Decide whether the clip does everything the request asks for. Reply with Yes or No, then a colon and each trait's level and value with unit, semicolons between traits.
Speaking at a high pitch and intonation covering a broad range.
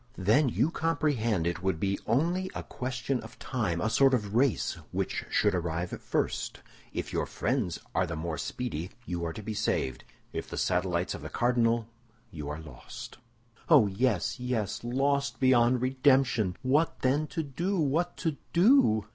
No: low, 120 Hz; wide, 7.0 semitones